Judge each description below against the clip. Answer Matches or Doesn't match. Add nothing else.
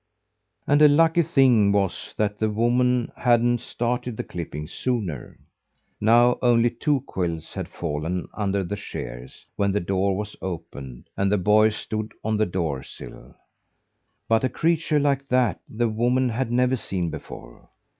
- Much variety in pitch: Doesn't match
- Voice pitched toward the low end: Matches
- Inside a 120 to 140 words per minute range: Doesn't match